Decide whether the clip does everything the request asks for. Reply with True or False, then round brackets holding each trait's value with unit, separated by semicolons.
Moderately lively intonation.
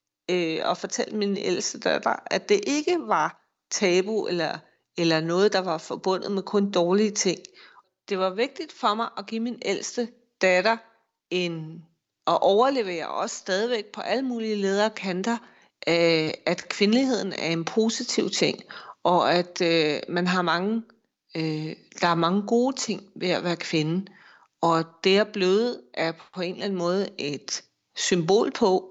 True (4.6 semitones)